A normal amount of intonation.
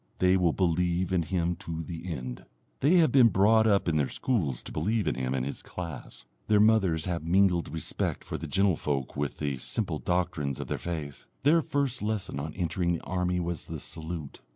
Yes: average, 4.0 semitones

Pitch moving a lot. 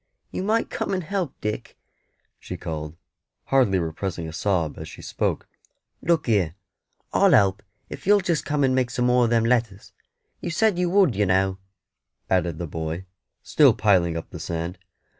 Yes: wide, 8.6 semitones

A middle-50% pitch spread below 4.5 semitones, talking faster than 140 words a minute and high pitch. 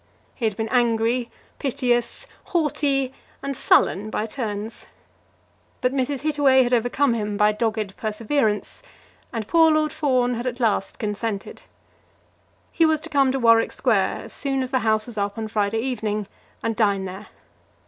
Yes: average, 3.9 semitones; average, 160 wpm; high, 235 Hz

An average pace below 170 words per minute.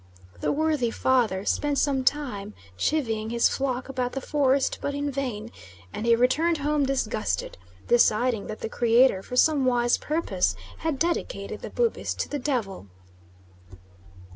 Yes: average, 145 wpm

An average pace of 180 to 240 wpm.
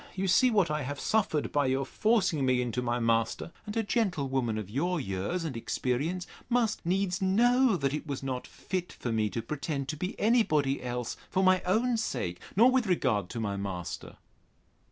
Yes: average, 195 wpm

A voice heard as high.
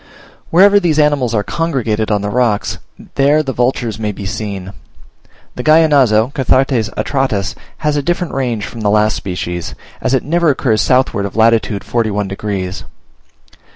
No: low, 115 Hz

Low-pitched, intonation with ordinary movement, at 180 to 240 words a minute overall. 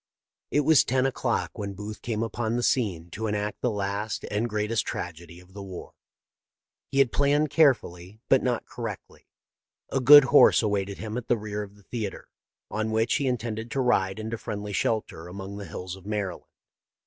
Yes: low, 110 Hz; average, 3.3 semitones; average, 185 wpm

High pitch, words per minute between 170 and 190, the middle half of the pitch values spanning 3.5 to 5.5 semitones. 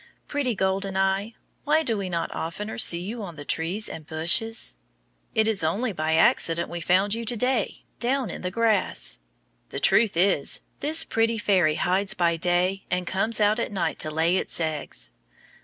Yes: high, 195 Hz; average, 180 wpm; average, 4.8 semitones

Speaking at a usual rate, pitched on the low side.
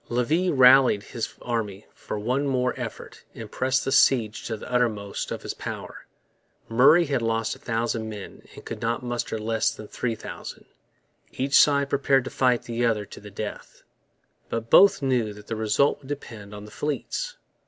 Yes: average, 180 wpm; low, 120 Hz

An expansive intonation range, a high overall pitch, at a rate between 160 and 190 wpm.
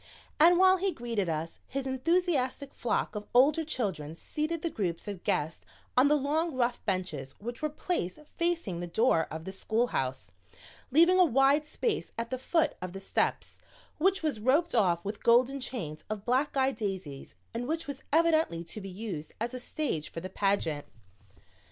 Yes: wide, 8.4 semitones; high, 245 Hz; average, 175 wpm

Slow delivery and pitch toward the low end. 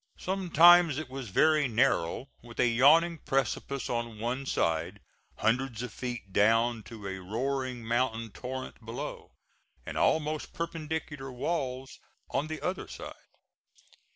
Yes: slow, 125 wpm; low, 130 Hz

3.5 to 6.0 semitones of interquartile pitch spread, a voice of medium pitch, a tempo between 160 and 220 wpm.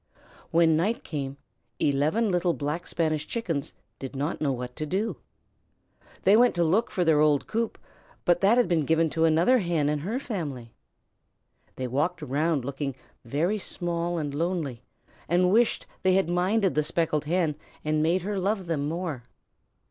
Yes: average, 3.9 semitones; medium, 165 Hz; average, 165 wpm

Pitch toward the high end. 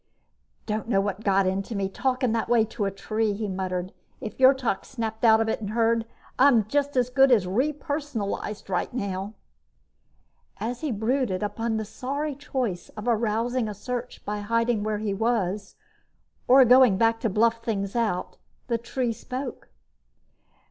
Yes: high, 225 Hz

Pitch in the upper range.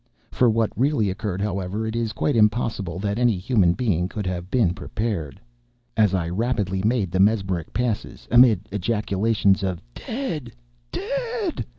No: low, 105 Hz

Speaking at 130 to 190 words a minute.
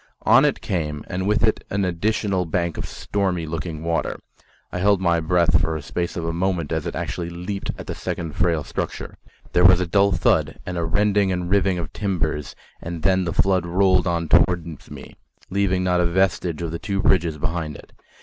No: fast, 205 wpm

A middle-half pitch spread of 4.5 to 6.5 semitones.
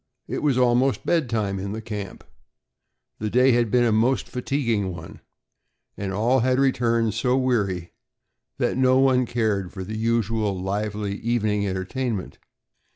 No: average, 3.7 semitones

